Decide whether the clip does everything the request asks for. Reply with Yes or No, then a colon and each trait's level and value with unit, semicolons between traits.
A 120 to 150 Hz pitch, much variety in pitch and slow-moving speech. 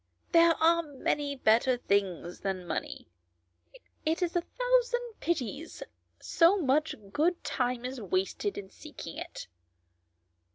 No: very high, 295 Hz; wide, 6.9 semitones; slow, 120 wpm